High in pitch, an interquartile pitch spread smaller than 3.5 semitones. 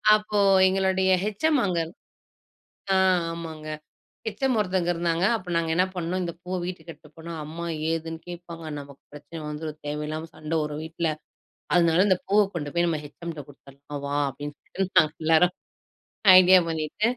No: medium, 165 Hz; average, 3.0 semitones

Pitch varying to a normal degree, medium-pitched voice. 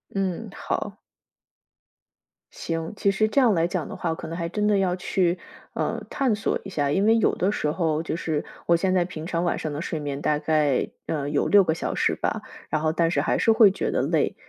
Yes: average, 3.7 semitones; medium, 170 Hz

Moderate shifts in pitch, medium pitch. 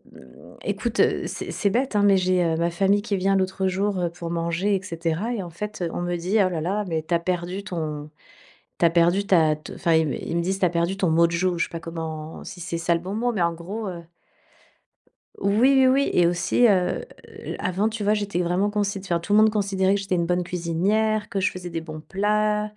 Yes: average, 3.2 semitones; medium, 180 Hz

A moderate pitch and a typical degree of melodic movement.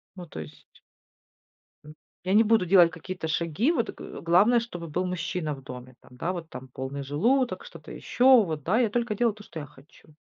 No: medium, 175 Hz; wide, 6.4 semitones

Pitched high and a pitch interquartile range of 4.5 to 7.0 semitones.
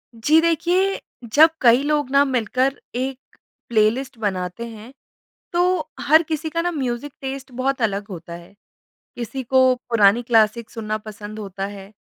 Yes: high, 245 Hz; average, 4.8 semitones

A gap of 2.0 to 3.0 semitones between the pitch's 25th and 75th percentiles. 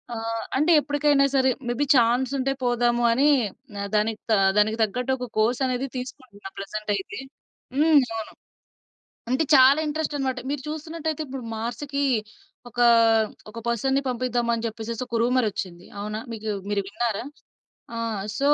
No: average, 3.5 semitones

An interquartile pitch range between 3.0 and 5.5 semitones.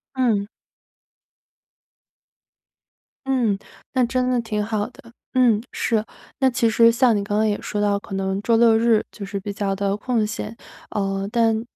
No: narrow, 2.5 semitones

